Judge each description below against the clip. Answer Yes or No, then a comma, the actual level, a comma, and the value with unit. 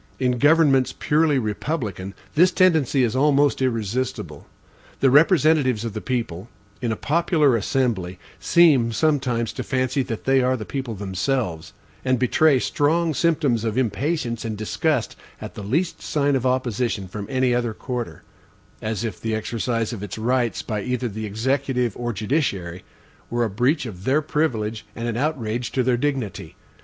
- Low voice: Yes, low, 125 Hz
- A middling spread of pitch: Yes, average, 4.1 semitones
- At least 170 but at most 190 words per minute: No, average, 160 wpm